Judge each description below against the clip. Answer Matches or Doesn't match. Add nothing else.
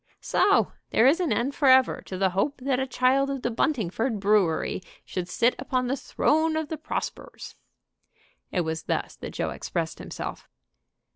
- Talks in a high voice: Matches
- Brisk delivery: Doesn't match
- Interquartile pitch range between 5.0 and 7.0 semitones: Matches